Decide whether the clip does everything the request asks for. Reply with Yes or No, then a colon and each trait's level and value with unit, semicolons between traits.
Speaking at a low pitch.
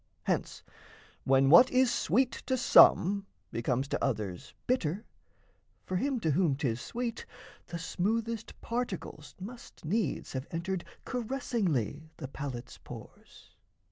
No: medium, 185 Hz